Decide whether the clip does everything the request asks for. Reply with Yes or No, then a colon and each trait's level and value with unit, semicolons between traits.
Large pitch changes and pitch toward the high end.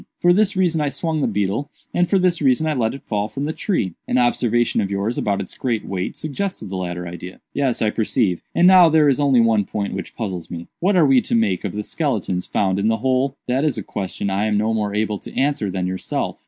No: wide, 6.5 semitones; low, 115 Hz